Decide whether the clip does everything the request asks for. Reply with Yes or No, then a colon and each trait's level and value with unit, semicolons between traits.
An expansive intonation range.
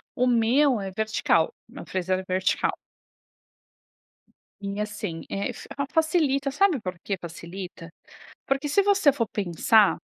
Yes: wide, 6.8 semitones